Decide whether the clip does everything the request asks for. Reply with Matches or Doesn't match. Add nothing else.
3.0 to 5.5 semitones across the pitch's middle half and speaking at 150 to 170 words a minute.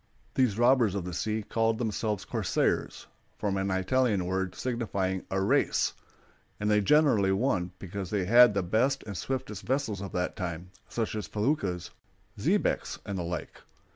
Matches